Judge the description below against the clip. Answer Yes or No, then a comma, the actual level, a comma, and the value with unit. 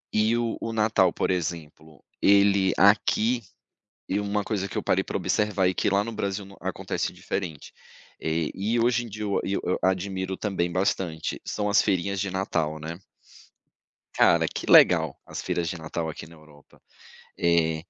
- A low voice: Yes, very low, 95 Hz